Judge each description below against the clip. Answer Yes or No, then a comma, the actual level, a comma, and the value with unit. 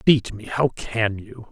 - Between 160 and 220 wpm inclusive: Yes, average, 200 wpm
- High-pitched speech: No, low, 115 Hz